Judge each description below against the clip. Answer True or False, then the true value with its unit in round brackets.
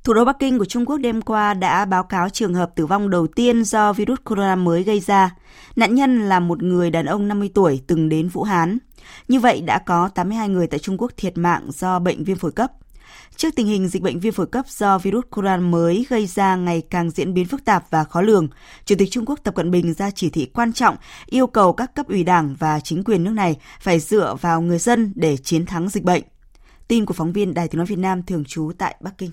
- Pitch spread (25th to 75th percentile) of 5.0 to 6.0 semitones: False (4.0 semitones)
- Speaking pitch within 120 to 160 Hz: False (190 Hz)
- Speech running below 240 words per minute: False (250 wpm)